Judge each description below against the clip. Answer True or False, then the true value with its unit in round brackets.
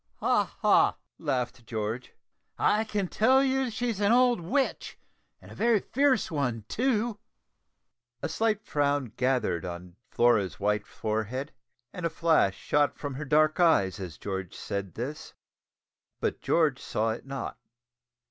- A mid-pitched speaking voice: True (145 Hz)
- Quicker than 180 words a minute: False (145 wpm)